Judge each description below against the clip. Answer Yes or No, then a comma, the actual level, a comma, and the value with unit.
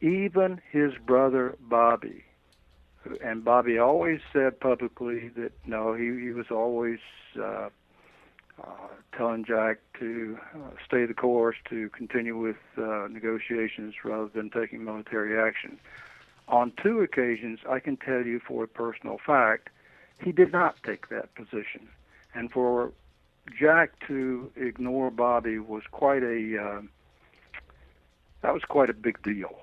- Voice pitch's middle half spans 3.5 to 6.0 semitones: No, narrow, 2.4 semitones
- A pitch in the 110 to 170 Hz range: Yes, low, 115 Hz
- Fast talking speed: No, slow, 135 wpm